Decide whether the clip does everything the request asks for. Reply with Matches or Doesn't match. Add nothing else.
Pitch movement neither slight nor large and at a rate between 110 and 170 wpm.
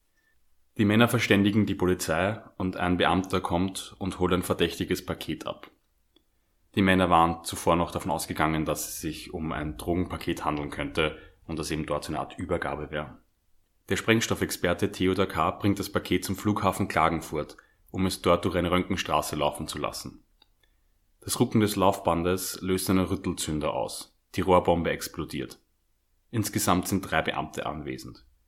Matches